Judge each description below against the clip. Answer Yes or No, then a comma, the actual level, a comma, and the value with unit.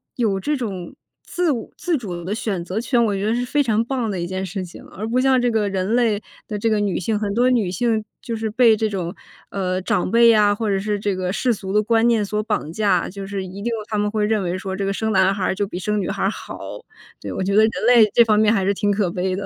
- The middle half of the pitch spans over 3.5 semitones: No, average, 2.9 semitones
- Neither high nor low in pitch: No, high, 210 Hz